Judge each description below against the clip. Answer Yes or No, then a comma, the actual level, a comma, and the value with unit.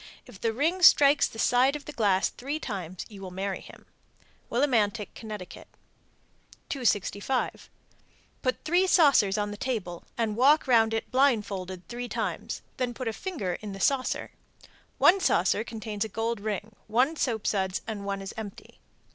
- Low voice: No, high, 225 Hz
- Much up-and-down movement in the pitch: No, average, 4.3 semitones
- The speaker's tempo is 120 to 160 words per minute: Yes, average, 155 wpm